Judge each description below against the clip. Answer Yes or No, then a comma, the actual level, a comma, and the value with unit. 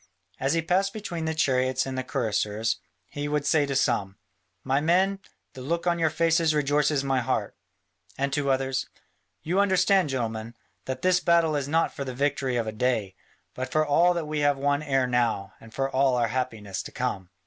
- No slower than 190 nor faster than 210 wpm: Yes, average, 195 wpm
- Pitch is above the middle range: No, medium, 140 Hz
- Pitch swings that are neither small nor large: Yes, average, 4.0 semitones